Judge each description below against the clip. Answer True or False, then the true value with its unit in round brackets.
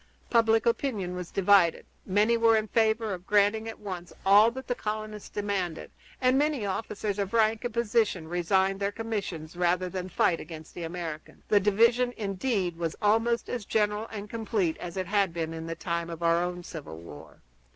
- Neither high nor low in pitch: False (200 Hz)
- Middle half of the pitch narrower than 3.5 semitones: False (4.1 semitones)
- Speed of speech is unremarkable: True (180 wpm)